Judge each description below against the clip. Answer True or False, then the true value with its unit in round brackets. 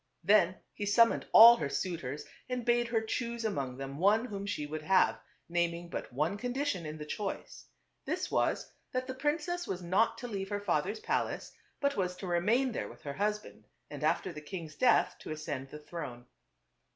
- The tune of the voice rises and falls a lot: True (6.9 semitones)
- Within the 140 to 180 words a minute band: False (190 wpm)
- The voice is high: True (195 Hz)